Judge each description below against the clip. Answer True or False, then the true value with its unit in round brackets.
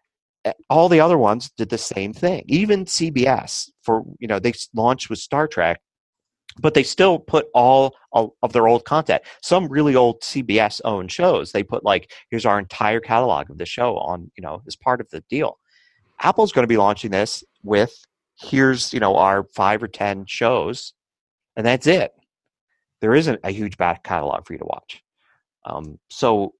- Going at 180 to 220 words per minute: True (185 wpm)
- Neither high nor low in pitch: False (120 Hz)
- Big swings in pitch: True (6.9 semitones)